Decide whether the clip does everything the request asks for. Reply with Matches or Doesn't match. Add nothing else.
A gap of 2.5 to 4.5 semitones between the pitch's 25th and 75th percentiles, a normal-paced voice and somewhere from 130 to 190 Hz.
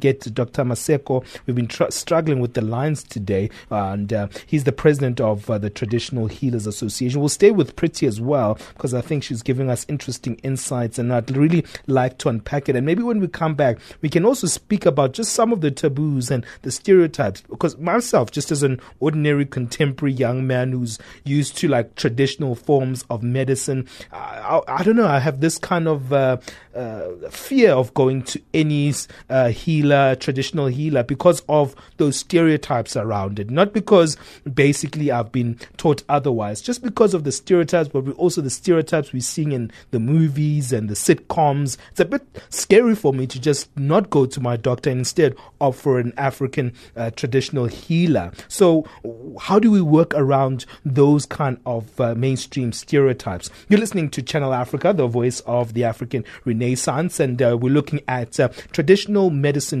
Matches